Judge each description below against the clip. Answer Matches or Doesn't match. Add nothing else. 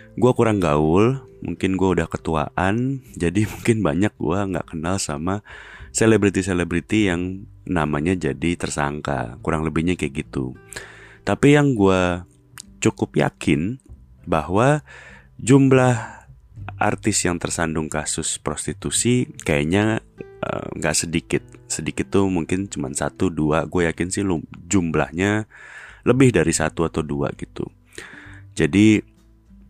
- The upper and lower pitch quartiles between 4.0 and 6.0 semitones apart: Matches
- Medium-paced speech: Matches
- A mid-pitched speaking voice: Doesn't match